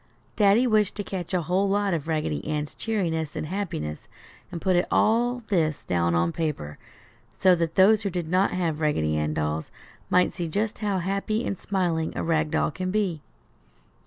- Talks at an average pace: Yes, average, 180 wpm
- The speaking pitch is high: No, medium, 175 Hz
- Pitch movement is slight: No, average, 4.6 semitones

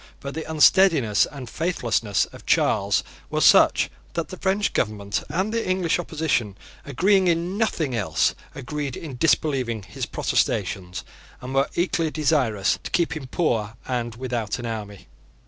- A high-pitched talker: No, low, 135 Hz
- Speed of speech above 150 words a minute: No, average, 145 wpm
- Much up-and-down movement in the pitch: Yes, wide, 6.8 semitones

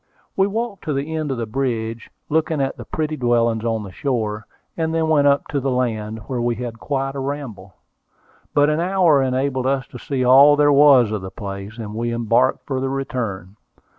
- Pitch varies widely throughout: No, average, 4.2 semitones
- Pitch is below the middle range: Yes, low, 130 Hz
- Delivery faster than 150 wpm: Yes, average, 200 wpm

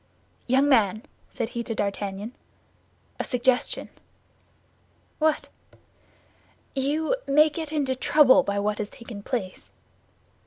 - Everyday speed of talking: No, slow, 110 wpm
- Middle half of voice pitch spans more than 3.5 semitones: Yes, wide, 5.4 semitones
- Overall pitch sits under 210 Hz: No, very high, 250 Hz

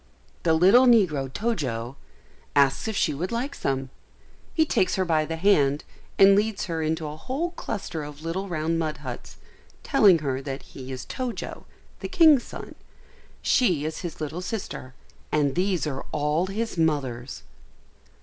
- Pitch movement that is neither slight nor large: No, wide, 5.9 semitones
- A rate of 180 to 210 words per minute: No, average, 160 wpm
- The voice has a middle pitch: Yes, medium, 160 Hz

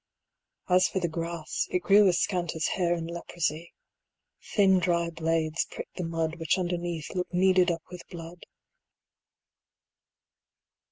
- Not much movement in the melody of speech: Yes, narrow, 1.6 semitones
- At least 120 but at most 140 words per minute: Yes, slow, 135 wpm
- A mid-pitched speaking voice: Yes, medium, 170 Hz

